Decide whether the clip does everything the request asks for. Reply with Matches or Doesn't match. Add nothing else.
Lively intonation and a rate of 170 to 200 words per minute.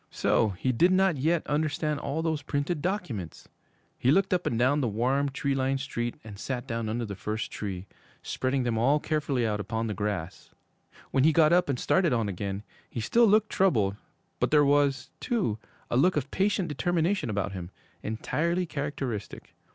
Matches